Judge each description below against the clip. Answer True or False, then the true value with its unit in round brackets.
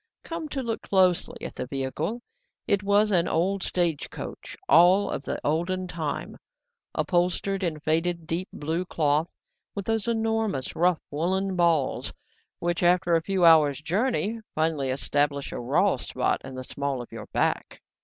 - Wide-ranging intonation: False (4.2 semitones)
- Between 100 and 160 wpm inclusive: True (155 wpm)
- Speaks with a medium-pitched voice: True (175 Hz)